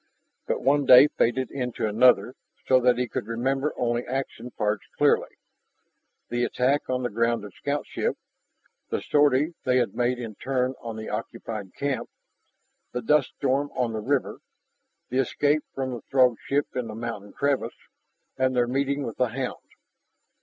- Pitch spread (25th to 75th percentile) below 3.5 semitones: Yes, narrow, 2.6 semitones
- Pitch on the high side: No, low, 125 Hz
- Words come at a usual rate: Yes, average, 160 wpm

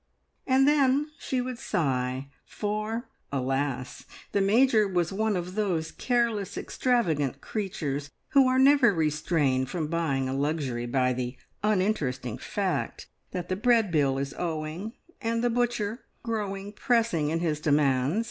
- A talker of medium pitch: Yes, medium, 180 Hz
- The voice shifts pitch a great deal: Yes, wide, 8.1 semitones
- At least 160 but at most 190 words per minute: No, average, 140 wpm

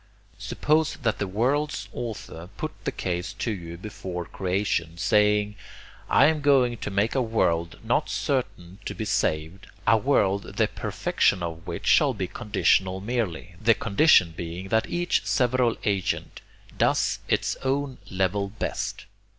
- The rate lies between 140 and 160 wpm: Yes, average, 145 wpm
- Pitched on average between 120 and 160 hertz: No, low, 105 Hz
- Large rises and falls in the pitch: No, average, 5.0 semitones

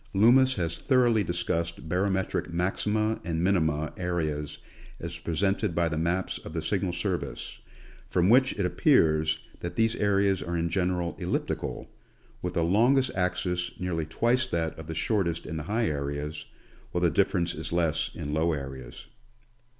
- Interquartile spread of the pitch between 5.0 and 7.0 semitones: No, average, 3.6 semitones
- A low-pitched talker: Yes, very low, 85 Hz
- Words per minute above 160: No, average, 155 wpm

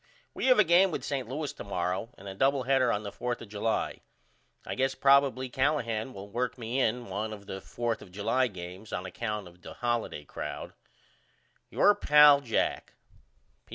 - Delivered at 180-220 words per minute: Yes, average, 185 wpm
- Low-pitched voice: Yes, low, 120 Hz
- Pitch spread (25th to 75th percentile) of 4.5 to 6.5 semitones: Yes, average, 4.8 semitones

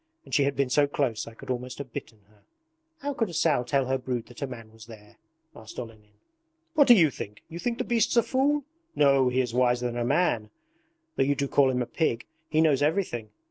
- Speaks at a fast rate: Yes, fast, 235 wpm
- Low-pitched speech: Yes, low, 130 Hz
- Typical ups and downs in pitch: Yes, average, 4.7 semitones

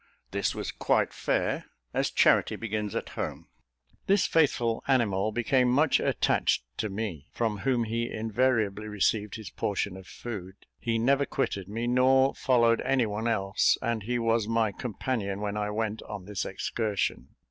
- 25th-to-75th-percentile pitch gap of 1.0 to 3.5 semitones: Yes, average, 2.9 semitones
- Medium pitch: No, low, 115 Hz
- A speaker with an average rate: Yes, average, 160 wpm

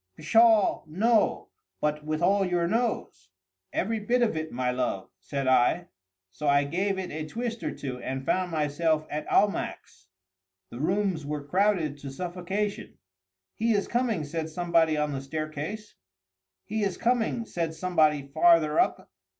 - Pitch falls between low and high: Yes, medium, 165 Hz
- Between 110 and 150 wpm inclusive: Yes, average, 145 wpm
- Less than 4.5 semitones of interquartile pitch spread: No, wide, 5.5 semitones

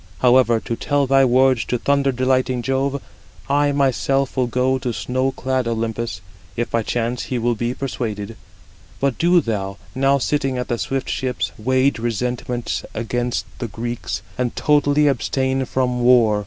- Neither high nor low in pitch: No, low, 125 Hz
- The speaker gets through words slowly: No, average, 155 wpm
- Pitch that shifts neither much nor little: No, narrow, 2.2 semitones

